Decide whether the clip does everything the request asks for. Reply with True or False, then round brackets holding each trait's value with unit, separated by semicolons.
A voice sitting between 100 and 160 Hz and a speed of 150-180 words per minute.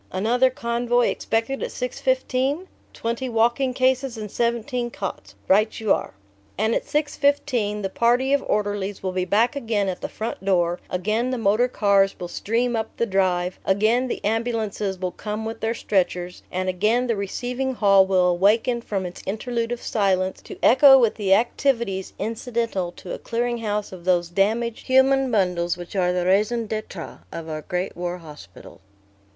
False (220 Hz; 170 wpm)